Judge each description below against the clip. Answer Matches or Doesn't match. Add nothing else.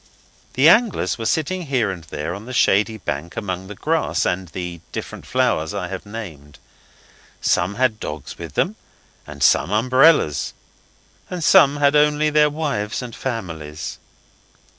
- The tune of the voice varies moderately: Doesn't match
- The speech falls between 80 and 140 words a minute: Doesn't match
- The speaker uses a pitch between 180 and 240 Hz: Doesn't match